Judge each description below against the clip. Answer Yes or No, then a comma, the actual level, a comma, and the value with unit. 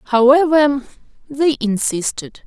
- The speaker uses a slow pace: Yes, slow, 75 wpm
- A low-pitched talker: No, very high, 265 Hz